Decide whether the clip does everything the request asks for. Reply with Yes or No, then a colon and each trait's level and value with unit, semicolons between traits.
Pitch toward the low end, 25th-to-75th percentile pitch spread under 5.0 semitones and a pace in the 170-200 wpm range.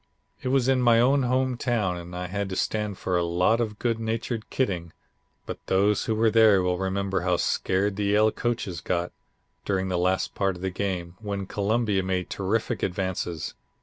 Yes: low, 100 Hz; average, 3.6 semitones; average, 190 wpm